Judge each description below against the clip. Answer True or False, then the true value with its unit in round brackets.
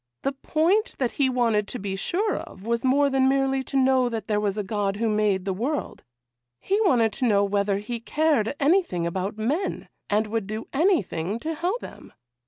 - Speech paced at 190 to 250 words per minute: True (195 wpm)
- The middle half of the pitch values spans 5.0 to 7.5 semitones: True (5.3 semitones)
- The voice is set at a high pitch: True (230 Hz)